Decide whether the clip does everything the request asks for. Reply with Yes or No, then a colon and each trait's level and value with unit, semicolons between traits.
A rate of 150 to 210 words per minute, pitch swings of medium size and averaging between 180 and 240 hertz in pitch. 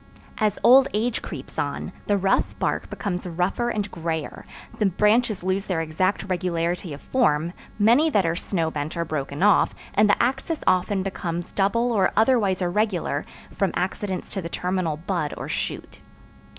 Yes: average, 165 wpm; average, 3.9 semitones; medium, 185 Hz